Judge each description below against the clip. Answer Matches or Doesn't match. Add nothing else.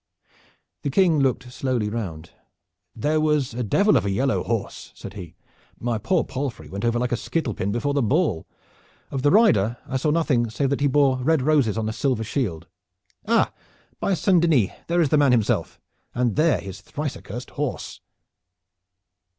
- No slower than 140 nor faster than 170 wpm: Doesn't match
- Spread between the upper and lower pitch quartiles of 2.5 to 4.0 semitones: Doesn't match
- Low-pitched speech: Matches